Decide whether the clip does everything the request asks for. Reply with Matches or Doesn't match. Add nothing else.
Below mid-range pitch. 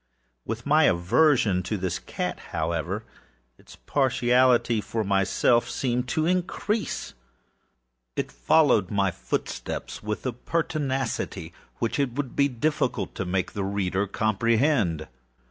Matches